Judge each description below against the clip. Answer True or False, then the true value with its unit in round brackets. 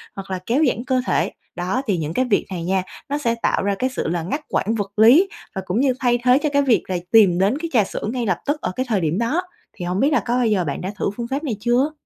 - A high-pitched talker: True (230 Hz)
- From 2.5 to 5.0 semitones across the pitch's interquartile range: False (5.4 semitones)